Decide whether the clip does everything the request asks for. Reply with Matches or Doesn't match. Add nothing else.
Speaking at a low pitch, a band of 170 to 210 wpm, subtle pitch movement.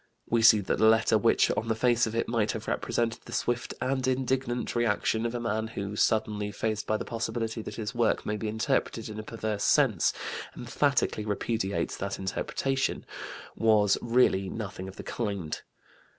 Matches